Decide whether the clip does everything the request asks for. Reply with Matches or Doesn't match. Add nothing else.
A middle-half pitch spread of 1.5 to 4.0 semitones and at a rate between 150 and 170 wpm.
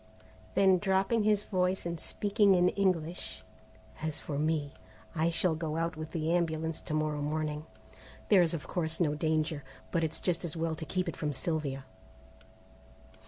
Matches